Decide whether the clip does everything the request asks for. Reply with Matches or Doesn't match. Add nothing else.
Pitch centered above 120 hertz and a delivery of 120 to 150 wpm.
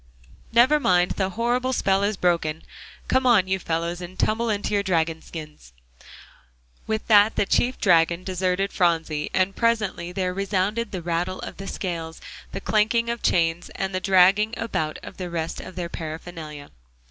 Doesn't match